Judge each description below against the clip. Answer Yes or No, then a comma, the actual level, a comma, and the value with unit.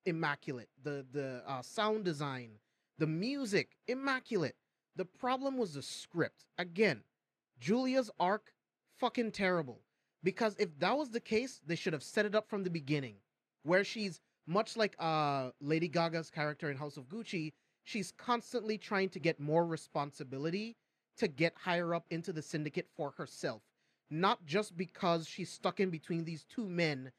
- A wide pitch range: Yes, wide, 5.9 semitones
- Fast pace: No, average, 160 wpm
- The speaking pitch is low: No, medium, 175 Hz